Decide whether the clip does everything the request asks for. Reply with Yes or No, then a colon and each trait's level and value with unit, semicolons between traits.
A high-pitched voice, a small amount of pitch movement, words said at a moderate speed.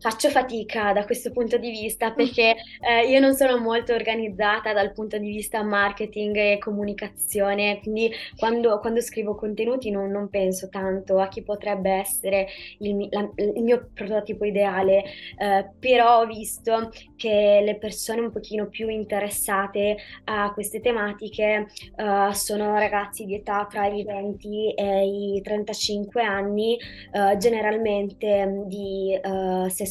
Yes: high, 210 Hz; narrow, 1.7 semitones; average, 140 wpm